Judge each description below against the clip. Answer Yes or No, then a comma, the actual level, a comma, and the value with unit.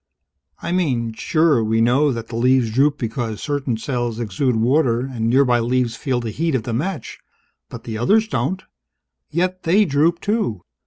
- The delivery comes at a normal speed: Yes, average, 170 wpm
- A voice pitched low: Yes, low, 130 Hz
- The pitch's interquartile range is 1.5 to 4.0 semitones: No, average, 5.1 semitones